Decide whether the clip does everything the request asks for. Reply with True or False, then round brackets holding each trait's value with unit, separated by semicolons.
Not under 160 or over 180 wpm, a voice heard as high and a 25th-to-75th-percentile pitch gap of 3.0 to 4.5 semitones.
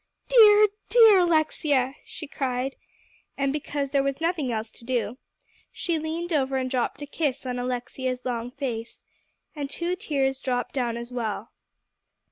False (150 wpm; 270 Hz; 3.9 semitones)